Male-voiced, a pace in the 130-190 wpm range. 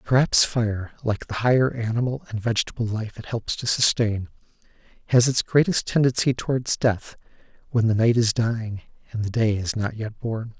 Yes: male; average, 175 wpm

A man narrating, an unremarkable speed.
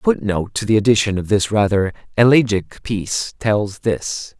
Yes: male; average, 165 wpm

